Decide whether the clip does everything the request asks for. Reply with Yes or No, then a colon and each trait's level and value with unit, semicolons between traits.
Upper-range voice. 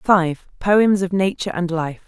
No: medium, 180 Hz